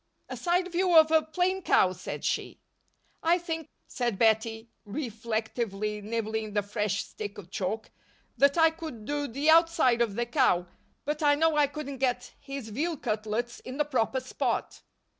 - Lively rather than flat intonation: Yes, wide, 6.3 semitones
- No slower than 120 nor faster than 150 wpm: No, average, 165 wpm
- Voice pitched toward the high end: Yes, very high, 255 Hz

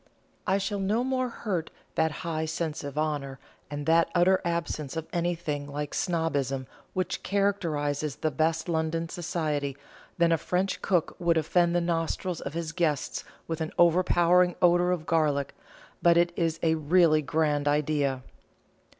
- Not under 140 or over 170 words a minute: Yes, average, 150 wpm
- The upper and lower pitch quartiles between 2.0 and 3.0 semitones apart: Yes, narrow, 2.6 semitones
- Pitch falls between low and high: Yes, medium, 165 Hz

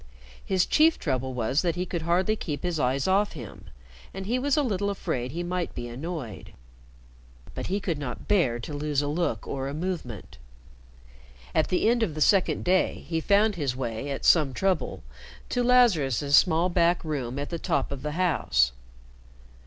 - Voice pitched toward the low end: No, medium, 160 Hz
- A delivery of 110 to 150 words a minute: No, average, 185 wpm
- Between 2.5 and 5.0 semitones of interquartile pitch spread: No, wide, 5.6 semitones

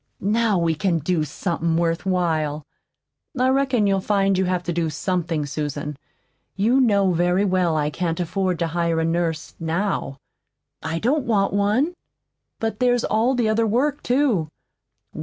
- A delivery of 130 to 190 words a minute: Yes, average, 155 wpm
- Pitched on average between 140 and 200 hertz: Yes, medium, 185 Hz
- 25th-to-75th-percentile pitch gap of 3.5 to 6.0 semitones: Yes, average, 4.8 semitones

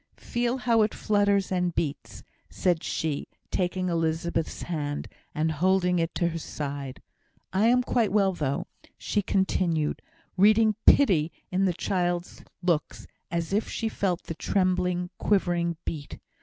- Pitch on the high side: No, medium, 180 Hz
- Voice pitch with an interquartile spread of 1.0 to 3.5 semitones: Yes, average, 3.2 semitones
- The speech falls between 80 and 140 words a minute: Yes, slow, 135 wpm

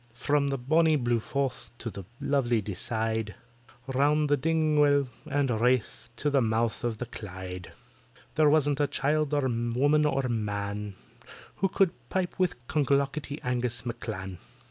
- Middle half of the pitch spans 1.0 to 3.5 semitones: No, average, 4.4 semitones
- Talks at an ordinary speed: Yes, average, 145 wpm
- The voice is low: Yes, low, 130 Hz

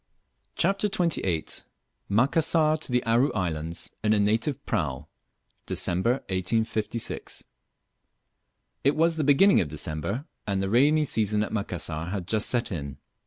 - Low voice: Yes, low, 110 Hz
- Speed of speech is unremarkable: No, slow, 130 wpm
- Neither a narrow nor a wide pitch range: No, wide, 8.2 semitones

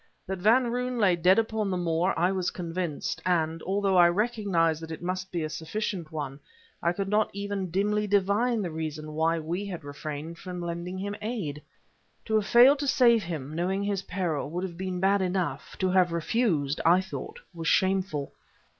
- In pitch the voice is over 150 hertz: Yes, medium, 185 Hz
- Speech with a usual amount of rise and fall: Yes, average, 3.5 semitones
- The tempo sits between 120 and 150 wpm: No, average, 190 wpm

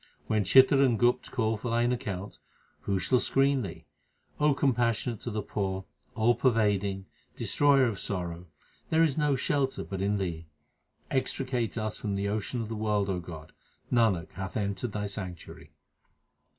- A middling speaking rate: Yes, average, 160 wpm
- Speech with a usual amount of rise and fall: Yes, average, 4.2 semitones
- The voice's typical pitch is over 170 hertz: No, low, 110 Hz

